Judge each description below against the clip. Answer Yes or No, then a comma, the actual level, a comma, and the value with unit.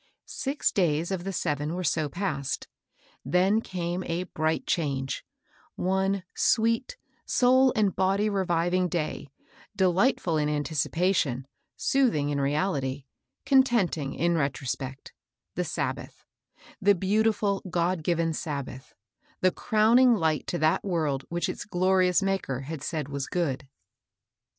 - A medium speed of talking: No, slow, 130 wpm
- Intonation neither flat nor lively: Yes, average, 4.7 semitones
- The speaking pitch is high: No, medium, 175 Hz